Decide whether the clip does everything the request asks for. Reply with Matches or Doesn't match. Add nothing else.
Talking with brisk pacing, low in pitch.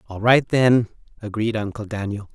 Doesn't match